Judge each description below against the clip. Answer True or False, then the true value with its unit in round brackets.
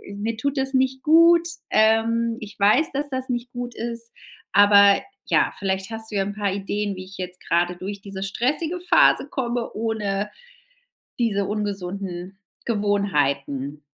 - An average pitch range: True (3.7 semitones)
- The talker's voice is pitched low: False (210 Hz)